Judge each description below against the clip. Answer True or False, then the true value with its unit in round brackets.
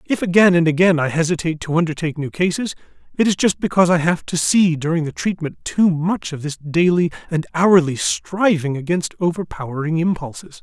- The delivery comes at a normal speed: True (180 wpm)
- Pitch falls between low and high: True (170 Hz)